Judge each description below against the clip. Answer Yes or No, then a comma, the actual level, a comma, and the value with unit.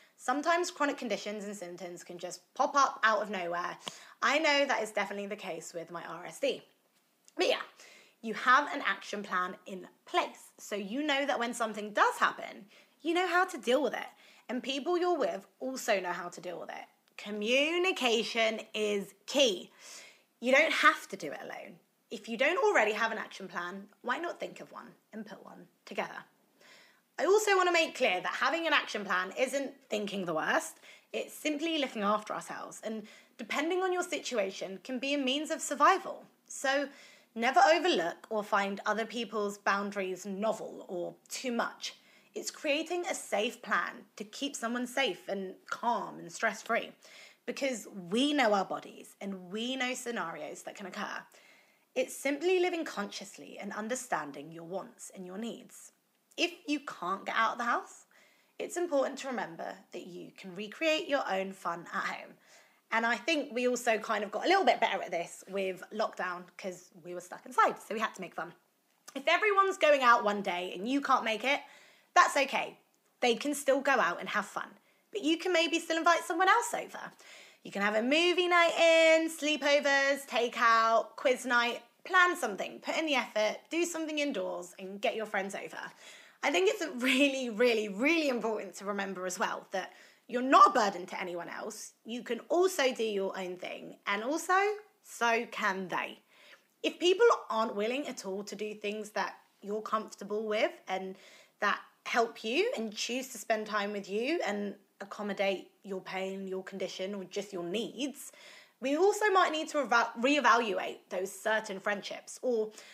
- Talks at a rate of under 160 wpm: No, average, 180 wpm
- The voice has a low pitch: No, high, 235 Hz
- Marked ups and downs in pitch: Yes, wide, 6.5 semitones